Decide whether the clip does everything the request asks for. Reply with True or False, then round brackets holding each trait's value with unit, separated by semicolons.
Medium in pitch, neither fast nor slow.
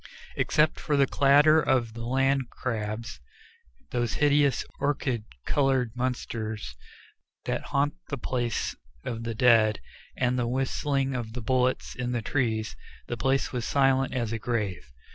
False (125 Hz; 145 wpm)